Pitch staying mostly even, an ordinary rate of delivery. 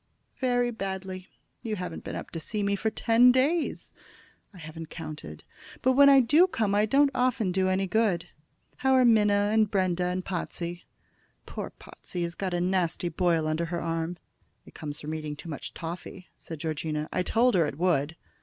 No: average, 5.0 semitones; average, 185 wpm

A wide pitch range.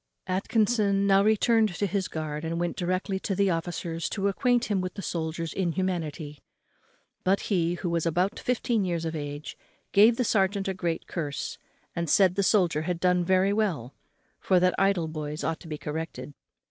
No: average, 3.4 semitones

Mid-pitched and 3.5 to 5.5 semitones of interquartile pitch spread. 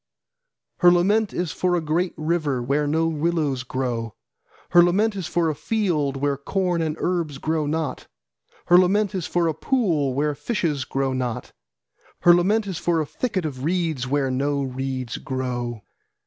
Yes: medium, 155 Hz; average, 4.5 semitones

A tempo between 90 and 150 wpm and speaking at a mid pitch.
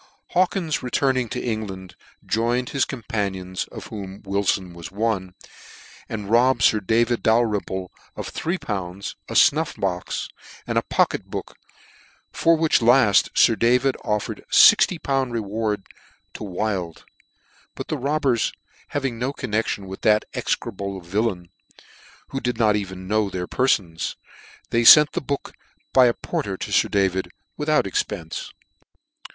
No: average, 140 wpm; low, 110 Hz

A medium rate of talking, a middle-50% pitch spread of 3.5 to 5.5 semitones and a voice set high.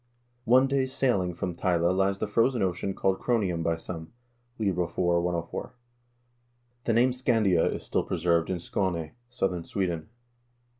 No: average, 155 wpm; average, 5.2 semitones; very low, 95 Hz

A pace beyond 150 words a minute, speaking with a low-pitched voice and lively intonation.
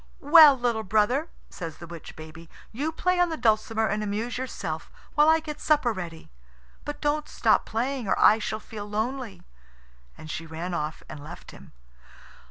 No: average, 175 wpm; high, 220 Hz; wide, 8.4 semitones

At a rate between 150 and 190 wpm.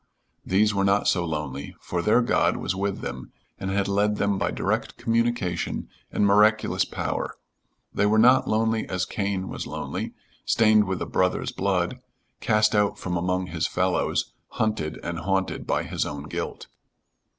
Yes: average, 160 wpm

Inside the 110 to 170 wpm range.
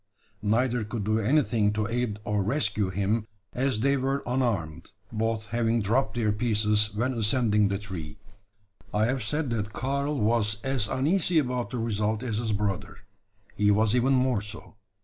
Yes: average, 165 wpm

